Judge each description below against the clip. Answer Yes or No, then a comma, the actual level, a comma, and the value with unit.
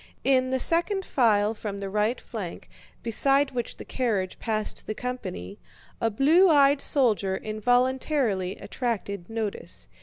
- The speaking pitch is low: No, high, 230 Hz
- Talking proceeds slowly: Yes, slow, 130 wpm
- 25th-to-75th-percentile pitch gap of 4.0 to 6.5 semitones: Yes, average, 4.4 semitones